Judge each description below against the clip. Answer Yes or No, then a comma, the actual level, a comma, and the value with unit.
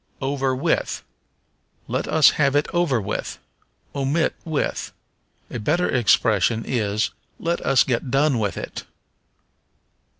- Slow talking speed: Yes, slow, 120 wpm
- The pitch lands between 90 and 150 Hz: Yes, low, 135 Hz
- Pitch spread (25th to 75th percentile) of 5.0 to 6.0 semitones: No, average, 4.4 semitones